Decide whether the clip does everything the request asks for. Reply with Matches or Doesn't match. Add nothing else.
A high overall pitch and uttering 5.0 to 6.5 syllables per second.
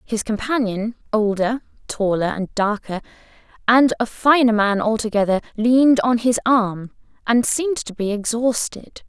Doesn't match